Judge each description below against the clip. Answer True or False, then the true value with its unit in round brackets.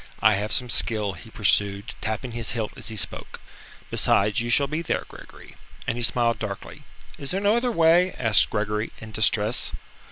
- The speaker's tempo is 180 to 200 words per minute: True (185 wpm)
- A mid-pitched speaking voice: False (115 Hz)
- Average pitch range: True (3.4 semitones)